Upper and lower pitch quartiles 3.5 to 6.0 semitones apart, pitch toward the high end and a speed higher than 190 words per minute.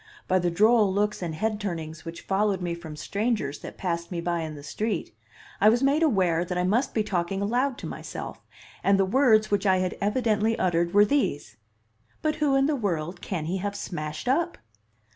Yes: average, 4.5 semitones; high, 195 Hz; average, 200 wpm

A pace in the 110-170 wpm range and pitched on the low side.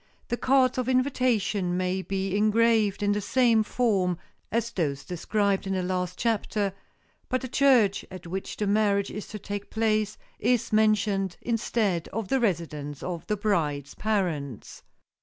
No: average, 155 wpm; high, 205 Hz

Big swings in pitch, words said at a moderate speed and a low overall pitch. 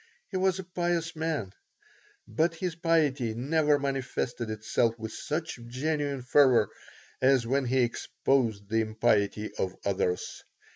No: wide, 6.1 semitones; slow, 130 wpm; low, 130 Hz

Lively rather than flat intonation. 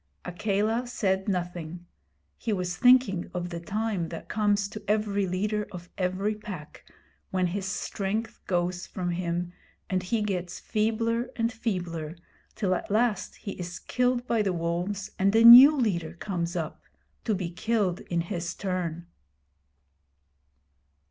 No: average, 3.5 semitones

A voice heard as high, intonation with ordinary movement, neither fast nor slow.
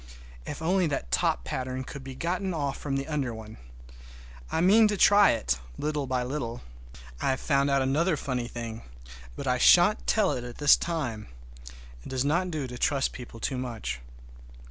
No: low, 135 Hz; average, 4.2 semitones; average, 180 wpm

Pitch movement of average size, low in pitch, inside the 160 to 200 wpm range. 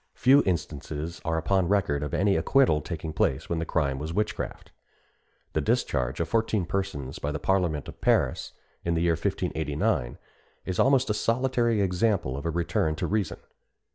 Yes: average, 5.0 semitones; very low, 85 Hz; average, 170 wpm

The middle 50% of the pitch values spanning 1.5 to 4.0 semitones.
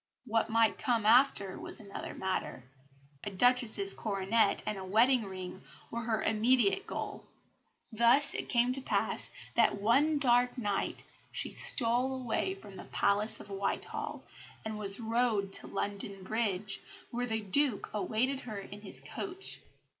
Yes: average, 3.6 semitones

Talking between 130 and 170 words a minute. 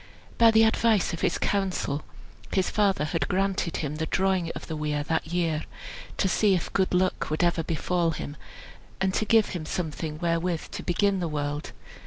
No: average, 185 wpm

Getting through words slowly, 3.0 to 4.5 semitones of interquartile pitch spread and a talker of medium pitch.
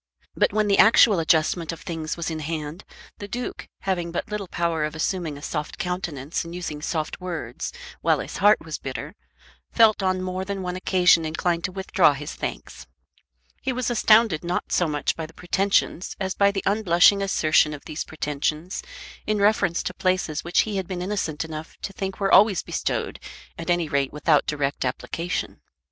No: average, 185 wpm; average, 3.9 semitones; medium, 175 Hz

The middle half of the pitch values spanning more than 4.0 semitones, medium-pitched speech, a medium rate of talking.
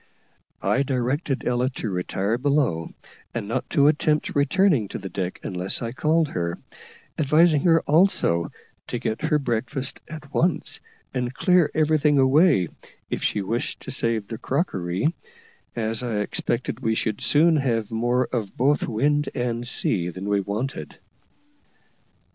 No: wide, 5.5 semitones; low, 125 Hz; average, 145 wpm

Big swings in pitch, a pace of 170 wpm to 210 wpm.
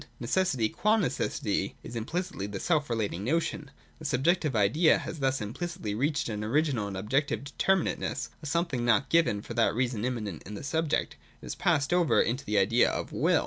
Yes: wide, 6.7 semitones; average, 195 wpm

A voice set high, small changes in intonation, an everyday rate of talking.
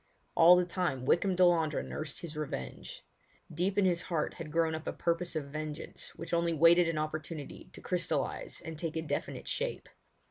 No: medium, 165 Hz; narrow, 2.1 semitones; average, 180 wpm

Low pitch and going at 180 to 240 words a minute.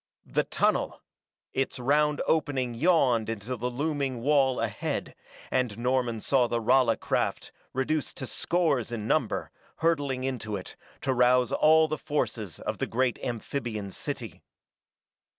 No: low, 130 Hz; slow, 135 wpm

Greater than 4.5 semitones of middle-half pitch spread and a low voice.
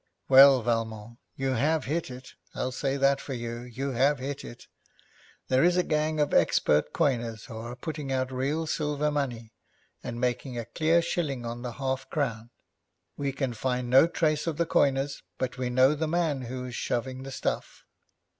No: average, 3.2 semitones; low, 130 Hz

